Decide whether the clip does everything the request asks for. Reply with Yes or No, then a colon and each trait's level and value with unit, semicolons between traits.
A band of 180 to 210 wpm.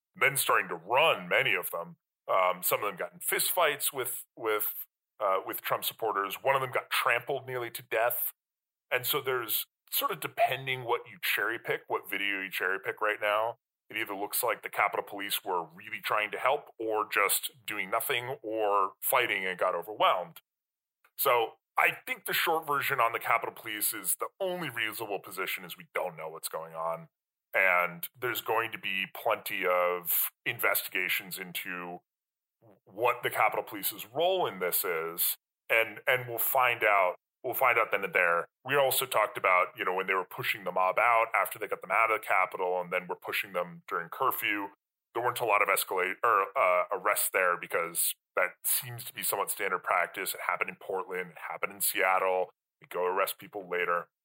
Yes: average, 190 wpm